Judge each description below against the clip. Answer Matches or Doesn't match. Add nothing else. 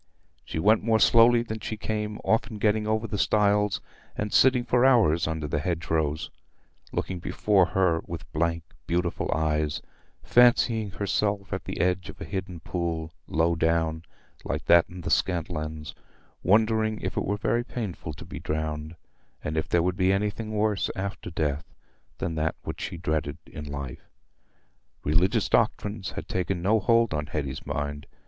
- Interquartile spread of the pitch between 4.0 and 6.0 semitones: Matches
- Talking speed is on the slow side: Doesn't match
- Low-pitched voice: Matches